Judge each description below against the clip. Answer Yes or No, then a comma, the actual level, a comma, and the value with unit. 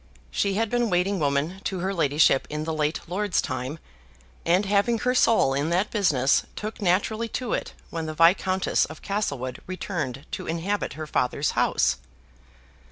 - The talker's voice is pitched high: No, medium, 175 Hz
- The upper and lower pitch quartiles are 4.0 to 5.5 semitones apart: Yes, average, 5.1 semitones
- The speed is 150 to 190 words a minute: Yes, average, 165 wpm